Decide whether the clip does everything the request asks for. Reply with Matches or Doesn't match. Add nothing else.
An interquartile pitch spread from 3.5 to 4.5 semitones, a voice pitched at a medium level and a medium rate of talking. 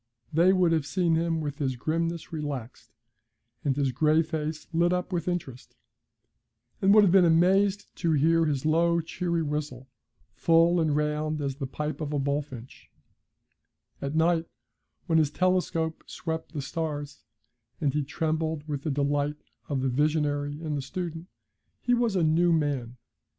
Doesn't match